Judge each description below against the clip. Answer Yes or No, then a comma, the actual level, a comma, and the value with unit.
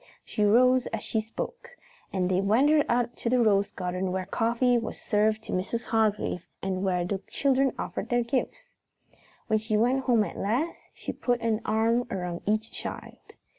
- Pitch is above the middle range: Yes, high, 225 Hz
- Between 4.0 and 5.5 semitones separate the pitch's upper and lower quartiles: No, average, 3.6 semitones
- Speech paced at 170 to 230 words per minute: Yes, average, 175 wpm